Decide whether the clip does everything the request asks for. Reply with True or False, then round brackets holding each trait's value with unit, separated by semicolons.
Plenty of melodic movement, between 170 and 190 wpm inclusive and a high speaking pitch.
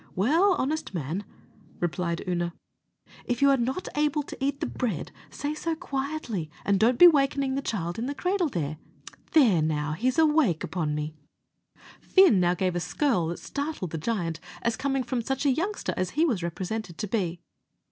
True (8.6 semitones; 175 wpm; 235 Hz)